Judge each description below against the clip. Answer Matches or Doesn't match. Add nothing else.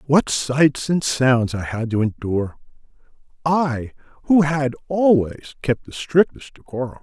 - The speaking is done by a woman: Doesn't match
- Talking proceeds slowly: Matches